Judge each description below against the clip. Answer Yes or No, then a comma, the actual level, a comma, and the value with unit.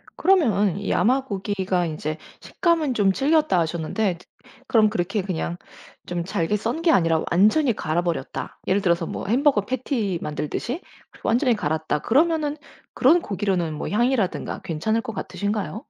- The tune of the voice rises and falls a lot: Yes, wide, 6.6 semitones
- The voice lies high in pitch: Yes, high, 205 Hz